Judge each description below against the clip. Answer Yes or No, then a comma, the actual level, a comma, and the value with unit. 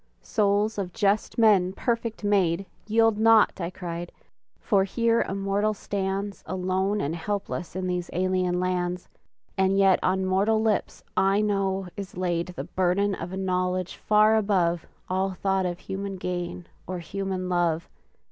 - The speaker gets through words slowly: No, average, 150 wpm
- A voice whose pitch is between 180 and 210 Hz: Yes, high, 190 Hz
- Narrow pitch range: Yes, narrow, 2.0 semitones